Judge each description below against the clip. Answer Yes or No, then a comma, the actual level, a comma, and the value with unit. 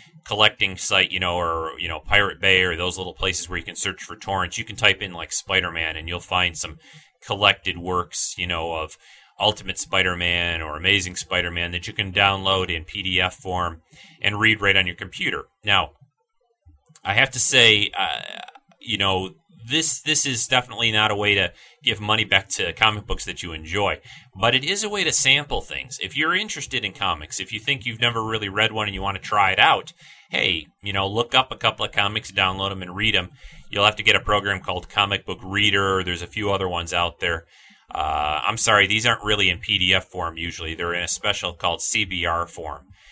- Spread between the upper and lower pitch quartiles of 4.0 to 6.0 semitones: No, average, 3.3 semitones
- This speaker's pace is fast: Yes, fast, 220 wpm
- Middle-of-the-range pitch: No, very low, 95 Hz